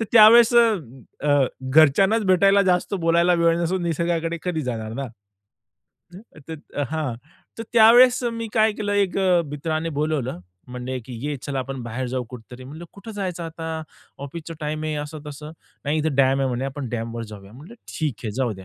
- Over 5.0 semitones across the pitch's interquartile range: Yes, wide, 5.4 semitones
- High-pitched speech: No, medium, 155 Hz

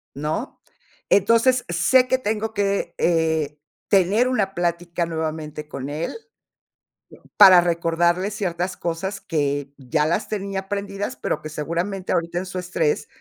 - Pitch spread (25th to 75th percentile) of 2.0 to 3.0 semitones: No, average, 3.8 semitones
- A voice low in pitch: No, medium, 175 Hz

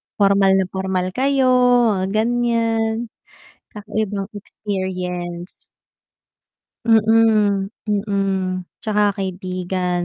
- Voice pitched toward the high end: Yes, high, 200 Hz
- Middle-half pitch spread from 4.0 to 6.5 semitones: No, average, 2.8 semitones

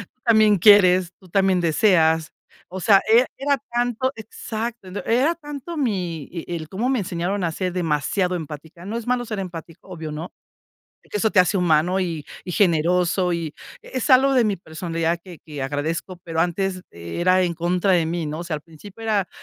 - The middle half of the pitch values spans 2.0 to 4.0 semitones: No, average, 4.4 semitones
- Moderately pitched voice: Yes, medium, 180 Hz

